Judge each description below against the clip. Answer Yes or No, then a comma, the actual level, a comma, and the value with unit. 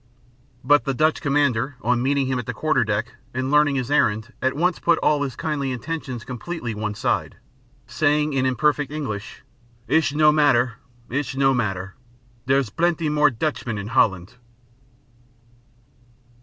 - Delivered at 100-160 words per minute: Yes, average, 150 wpm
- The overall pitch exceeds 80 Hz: Yes, low, 135 Hz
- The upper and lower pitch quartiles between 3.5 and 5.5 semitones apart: Yes, average, 3.9 semitones